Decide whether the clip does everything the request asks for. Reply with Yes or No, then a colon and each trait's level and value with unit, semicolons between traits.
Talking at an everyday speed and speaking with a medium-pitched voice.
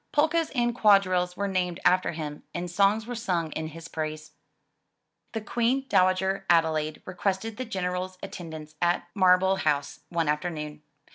Yes: average, 150 wpm; medium, 180 Hz